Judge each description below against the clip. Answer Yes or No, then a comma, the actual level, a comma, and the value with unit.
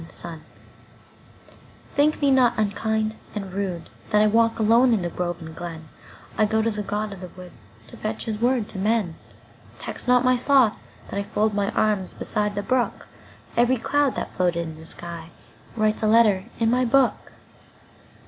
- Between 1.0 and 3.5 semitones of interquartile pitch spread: No, average, 4.4 semitones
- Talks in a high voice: Yes, high, 210 Hz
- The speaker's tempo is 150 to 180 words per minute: Yes, average, 160 wpm